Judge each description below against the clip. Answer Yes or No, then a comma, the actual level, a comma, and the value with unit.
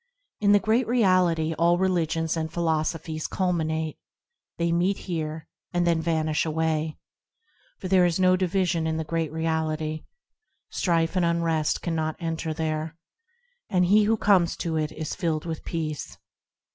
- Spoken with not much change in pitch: Yes, narrow, 2.1 semitones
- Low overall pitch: No, medium, 165 Hz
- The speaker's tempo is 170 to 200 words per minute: No, average, 145 wpm